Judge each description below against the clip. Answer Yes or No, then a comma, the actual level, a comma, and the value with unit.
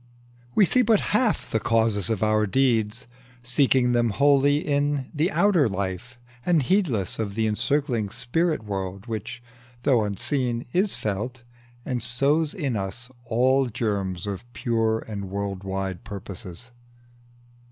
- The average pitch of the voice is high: No, low, 120 Hz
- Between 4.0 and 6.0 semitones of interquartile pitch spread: Yes, average, 5.2 semitones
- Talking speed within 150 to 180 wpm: No, slow, 135 wpm